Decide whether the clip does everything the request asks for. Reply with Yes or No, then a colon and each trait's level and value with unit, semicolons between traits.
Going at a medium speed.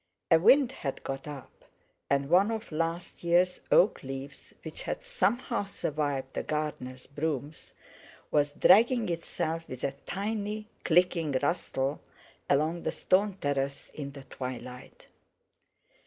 No: slow, 125 wpm